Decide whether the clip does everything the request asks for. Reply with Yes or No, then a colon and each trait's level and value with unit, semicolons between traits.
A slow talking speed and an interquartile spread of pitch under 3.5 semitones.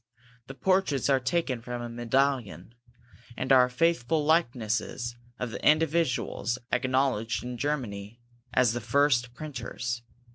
Yes: slow, 120 wpm; average, 3.1 semitones